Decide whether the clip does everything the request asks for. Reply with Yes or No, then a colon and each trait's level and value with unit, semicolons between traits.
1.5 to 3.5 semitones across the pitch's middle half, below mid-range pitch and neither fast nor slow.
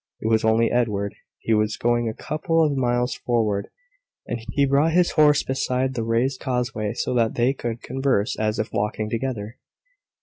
Yes: average, 3.2 semitones; low, 120 Hz; average, 175 wpm